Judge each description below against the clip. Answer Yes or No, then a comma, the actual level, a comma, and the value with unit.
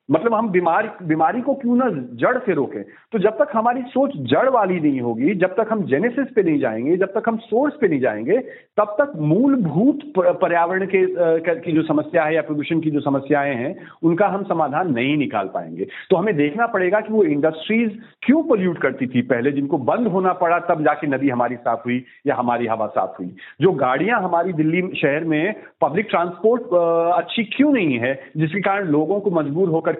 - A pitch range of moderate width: No, wide, 6.4 semitones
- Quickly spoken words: Yes, fast, 200 wpm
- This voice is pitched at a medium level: Yes, medium, 175 Hz